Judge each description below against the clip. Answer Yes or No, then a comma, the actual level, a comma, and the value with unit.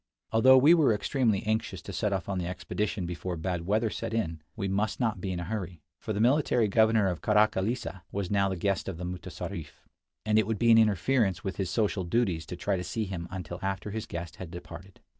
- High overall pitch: No, low, 100 Hz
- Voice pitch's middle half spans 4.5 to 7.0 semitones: No, average, 3.7 semitones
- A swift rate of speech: Yes, fast, 225 wpm